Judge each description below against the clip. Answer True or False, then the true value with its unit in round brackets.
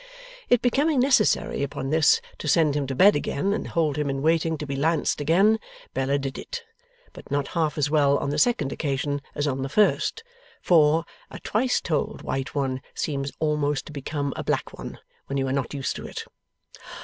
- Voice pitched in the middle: True (150 Hz)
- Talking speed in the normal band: True (195 wpm)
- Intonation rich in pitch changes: False (3.0 semitones)